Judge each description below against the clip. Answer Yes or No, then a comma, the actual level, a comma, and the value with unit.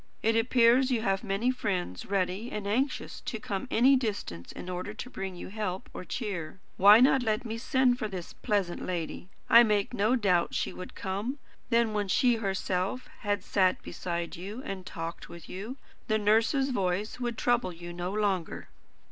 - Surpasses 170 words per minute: Yes, average, 180 wpm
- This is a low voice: No, high, 205 Hz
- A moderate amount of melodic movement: Yes, average, 4.2 semitones